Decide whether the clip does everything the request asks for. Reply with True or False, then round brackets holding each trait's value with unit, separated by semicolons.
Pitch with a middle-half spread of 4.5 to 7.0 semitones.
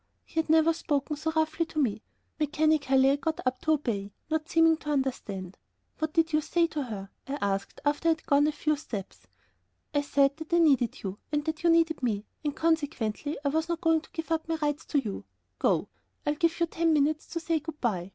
False (3.0 semitones)